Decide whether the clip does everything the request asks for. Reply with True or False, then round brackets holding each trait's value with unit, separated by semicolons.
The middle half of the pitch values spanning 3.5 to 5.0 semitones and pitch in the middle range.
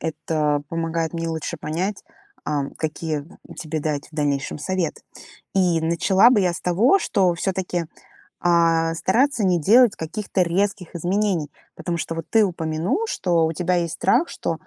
False (2.9 semitones; 170 Hz)